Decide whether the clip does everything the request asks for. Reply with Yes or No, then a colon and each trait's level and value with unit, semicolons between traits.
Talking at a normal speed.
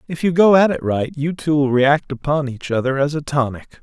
No: fast, 250 wpm